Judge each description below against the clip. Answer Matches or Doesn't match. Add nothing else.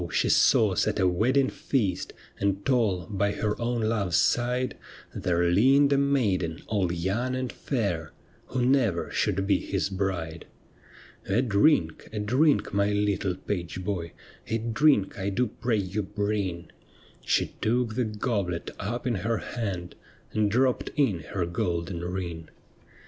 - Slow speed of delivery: Doesn't match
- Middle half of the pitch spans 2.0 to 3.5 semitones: Doesn't match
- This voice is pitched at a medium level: Doesn't match